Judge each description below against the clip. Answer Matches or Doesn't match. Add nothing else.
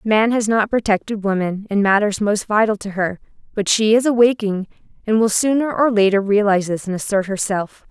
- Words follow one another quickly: Doesn't match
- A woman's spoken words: Matches